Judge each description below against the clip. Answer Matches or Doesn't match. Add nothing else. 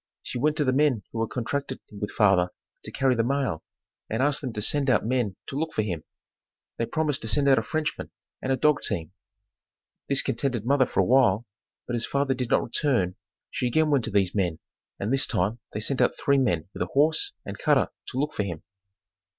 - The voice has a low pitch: Matches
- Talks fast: Matches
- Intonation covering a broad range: Doesn't match